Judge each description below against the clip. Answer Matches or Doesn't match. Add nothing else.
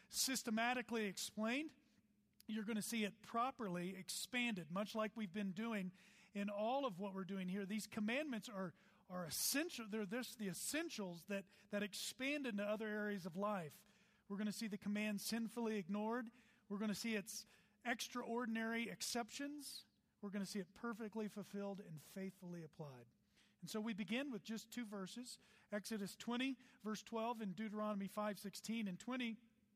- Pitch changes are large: Doesn't match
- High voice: Matches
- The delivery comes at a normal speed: Matches